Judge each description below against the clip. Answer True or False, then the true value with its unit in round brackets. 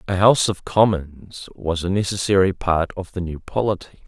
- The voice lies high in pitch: False (95 Hz)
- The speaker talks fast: False (175 wpm)